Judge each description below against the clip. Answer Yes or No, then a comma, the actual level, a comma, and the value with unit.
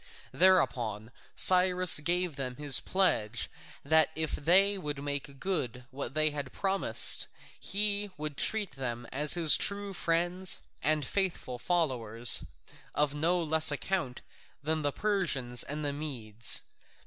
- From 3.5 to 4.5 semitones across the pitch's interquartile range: No, wide, 5.4 semitones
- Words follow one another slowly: Yes, slow, 125 wpm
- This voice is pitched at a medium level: Yes, medium, 150 Hz